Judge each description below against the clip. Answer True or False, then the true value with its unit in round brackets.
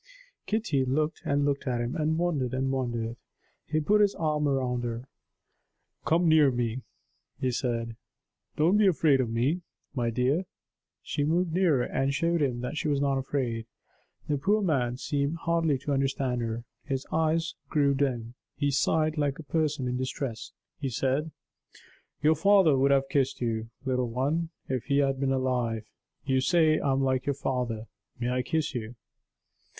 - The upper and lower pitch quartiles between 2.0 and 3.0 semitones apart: False (3.7 semitones)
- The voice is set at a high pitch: False (135 Hz)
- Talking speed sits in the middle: True (170 wpm)